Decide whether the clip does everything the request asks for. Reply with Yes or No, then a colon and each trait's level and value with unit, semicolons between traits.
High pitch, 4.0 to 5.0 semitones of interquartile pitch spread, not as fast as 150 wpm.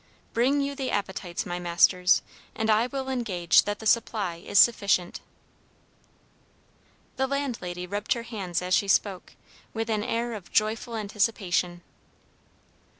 Yes: high, 210 Hz; average, 4.5 semitones; slow, 135 wpm